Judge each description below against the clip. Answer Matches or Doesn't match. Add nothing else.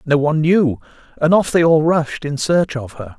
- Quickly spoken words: Matches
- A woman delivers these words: Doesn't match